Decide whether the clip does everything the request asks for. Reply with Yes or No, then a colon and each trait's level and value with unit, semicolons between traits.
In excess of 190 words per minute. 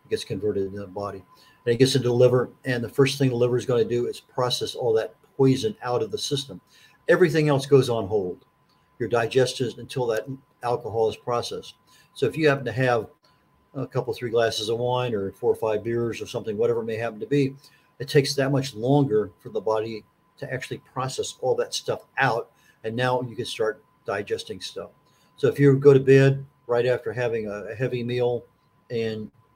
Yes: fast, 205 wpm